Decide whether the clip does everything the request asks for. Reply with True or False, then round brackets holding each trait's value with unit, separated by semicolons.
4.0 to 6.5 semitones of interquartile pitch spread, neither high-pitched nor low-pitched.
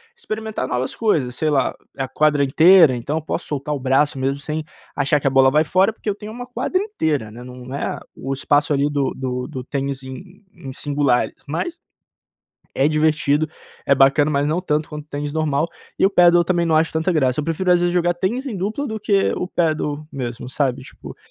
True (4.3 semitones; 150 Hz)